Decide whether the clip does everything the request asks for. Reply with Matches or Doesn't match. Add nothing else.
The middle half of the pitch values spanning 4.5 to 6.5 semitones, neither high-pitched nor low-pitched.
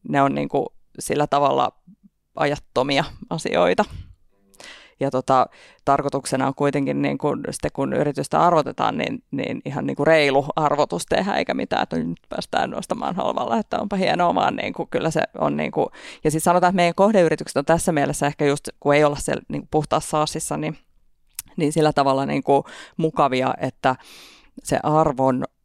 Doesn't match